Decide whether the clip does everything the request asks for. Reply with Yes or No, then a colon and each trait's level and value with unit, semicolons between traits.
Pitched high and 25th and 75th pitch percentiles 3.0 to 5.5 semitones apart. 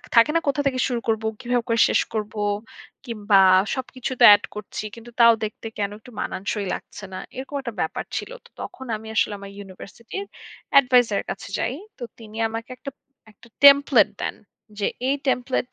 Yes: high, 230 Hz; average, 3.4 semitones